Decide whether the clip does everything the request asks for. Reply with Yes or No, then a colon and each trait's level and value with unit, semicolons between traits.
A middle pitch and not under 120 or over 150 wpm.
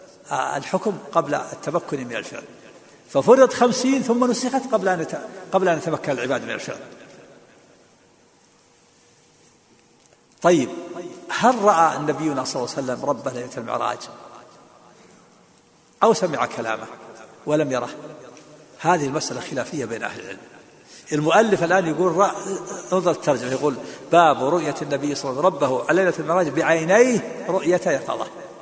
Yes: medium, 165 Hz; average, 125 wpm